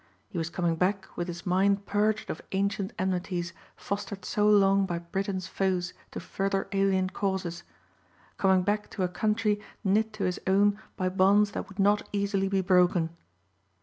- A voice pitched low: No, high, 195 Hz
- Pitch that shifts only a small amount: Yes, narrow, 1.8 semitones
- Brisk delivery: No, average, 165 wpm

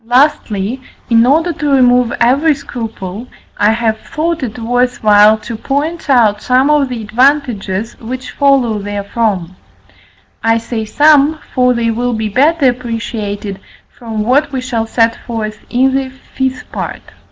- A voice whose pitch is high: Yes, high, 245 Hz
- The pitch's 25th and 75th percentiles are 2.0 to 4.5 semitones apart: Yes, average, 3.6 semitones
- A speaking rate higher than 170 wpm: No, average, 145 wpm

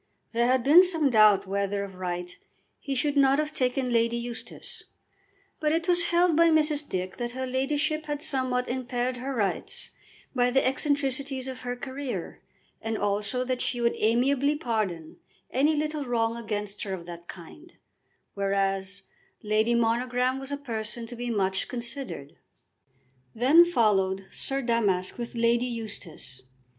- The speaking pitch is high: Yes, high, 245 Hz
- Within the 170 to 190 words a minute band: No, average, 150 wpm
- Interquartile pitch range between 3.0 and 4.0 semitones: No, average, 4.6 semitones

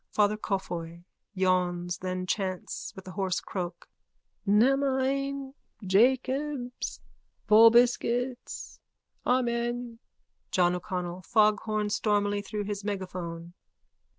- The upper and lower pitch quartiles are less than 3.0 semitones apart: No, average, 4.8 semitones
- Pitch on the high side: Yes, high, 205 Hz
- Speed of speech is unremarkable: No, slow, 90 wpm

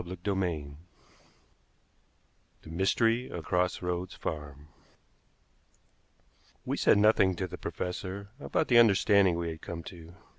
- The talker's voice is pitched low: Yes, very low, 90 Hz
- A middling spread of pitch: Yes, average, 3.0 semitones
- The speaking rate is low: Yes, slow, 120 wpm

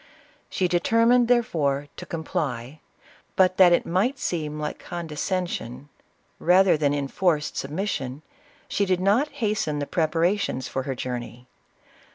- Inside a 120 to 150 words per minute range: Yes, average, 140 wpm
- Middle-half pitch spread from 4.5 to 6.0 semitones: Yes, average, 5.0 semitones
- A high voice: No, medium, 170 Hz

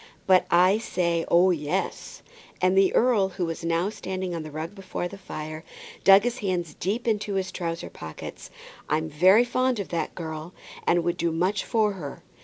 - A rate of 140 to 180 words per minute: No, average, 190 wpm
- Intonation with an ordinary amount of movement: Yes, average, 3.0 semitones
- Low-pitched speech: No, medium, 180 Hz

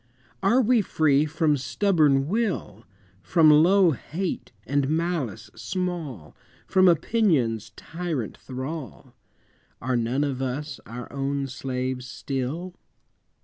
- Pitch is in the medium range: Yes, medium, 145 Hz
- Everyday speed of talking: No, slow, 105 wpm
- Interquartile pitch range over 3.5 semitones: Yes, average, 5.2 semitones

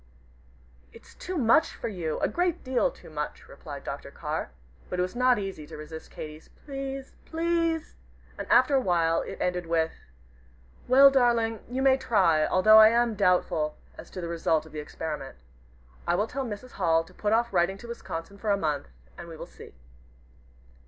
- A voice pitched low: No, high, 200 Hz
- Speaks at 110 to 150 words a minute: No, average, 185 wpm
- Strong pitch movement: Yes, wide, 7.6 semitones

